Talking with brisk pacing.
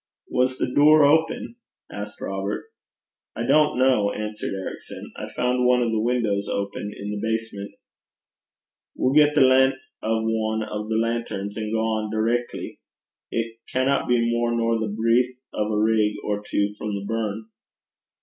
No: average, 160 wpm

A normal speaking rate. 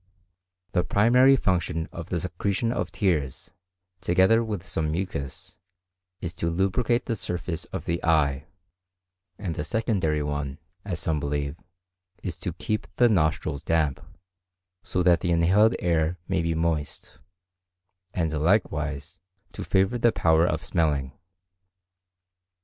No: slow, 130 wpm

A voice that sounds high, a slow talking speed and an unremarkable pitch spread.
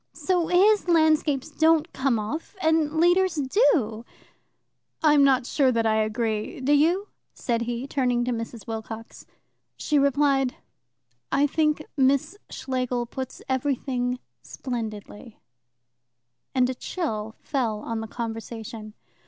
Yes: very high, 260 Hz; slow, 125 wpm; average, 4.8 semitones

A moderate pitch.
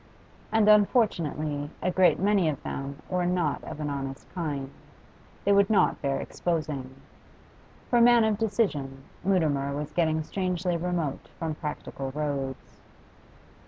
Yes: medium, 160 Hz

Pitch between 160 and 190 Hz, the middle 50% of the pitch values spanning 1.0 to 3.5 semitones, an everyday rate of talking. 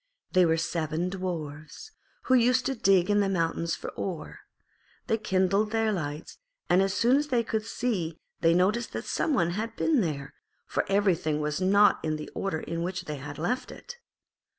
No: medium, 185 Hz; average, 4.9 semitones; average, 185 wpm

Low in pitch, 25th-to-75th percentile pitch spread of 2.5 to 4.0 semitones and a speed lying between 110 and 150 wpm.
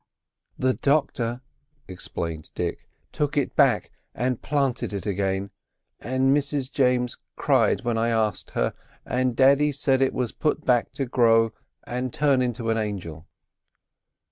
Yes: low, 125 Hz; average, 3.2 semitones; average, 140 wpm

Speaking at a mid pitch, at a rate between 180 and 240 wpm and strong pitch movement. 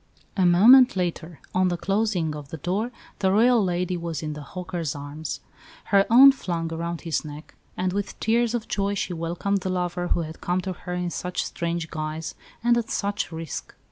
No: medium, 180 Hz; average, 195 wpm; average, 3.4 semitones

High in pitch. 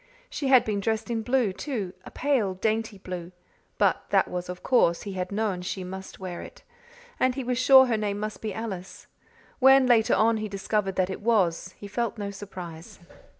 Yes: high, 210 Hz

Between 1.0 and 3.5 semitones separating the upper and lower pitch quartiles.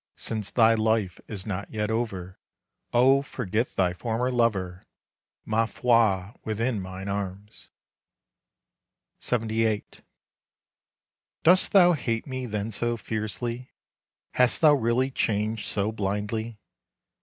Yes: average, 2.7 semitones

